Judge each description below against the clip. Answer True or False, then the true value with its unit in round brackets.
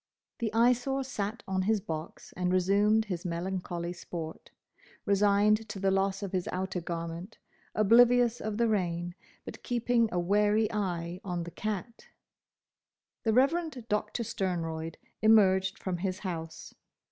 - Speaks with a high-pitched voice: True (195 Hz)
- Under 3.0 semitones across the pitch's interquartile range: False (3.8 semitones)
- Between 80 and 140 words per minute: True (135 wpm)